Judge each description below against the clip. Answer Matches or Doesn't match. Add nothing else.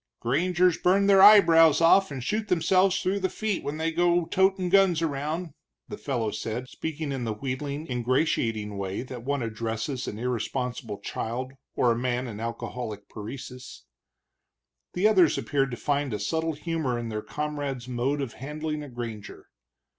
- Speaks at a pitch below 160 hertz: Matches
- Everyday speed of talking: Matches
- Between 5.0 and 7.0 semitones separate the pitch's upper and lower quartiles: Matches